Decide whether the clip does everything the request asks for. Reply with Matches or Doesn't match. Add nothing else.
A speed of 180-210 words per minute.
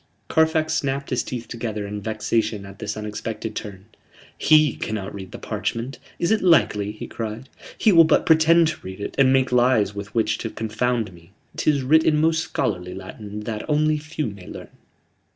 Matches